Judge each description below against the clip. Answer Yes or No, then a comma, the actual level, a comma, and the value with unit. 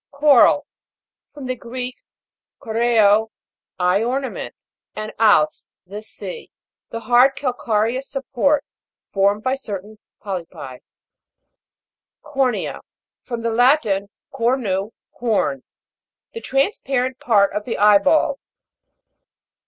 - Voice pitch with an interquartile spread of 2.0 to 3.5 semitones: No, average, 4.2 semitones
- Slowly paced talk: Yes, slow, 100 wpm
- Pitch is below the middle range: No, high, 230 Hz